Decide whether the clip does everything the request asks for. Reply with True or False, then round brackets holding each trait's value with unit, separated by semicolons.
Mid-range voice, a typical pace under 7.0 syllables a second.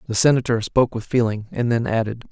False (115 Hz; 6.3 syllables/s)